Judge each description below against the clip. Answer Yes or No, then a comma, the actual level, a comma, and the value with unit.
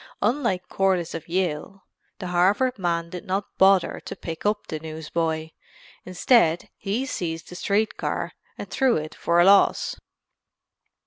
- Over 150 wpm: No, average, 145 wpm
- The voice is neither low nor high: Yes, medium, 180 Hz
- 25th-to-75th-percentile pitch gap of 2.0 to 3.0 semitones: No, average, 3.4 semitones